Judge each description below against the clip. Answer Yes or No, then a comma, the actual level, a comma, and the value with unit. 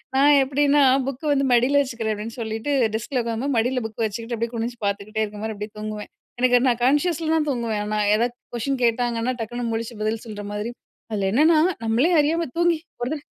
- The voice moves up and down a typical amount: Yes, average, 3.9 semitones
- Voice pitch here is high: Yes, high, 235 Hz